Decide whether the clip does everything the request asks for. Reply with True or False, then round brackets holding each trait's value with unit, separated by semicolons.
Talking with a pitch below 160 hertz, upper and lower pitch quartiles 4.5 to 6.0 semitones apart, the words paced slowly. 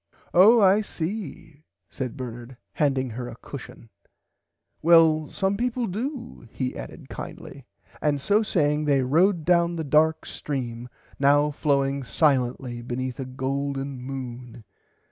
True (140 Hz; 4.8 semitones; 125 wpm)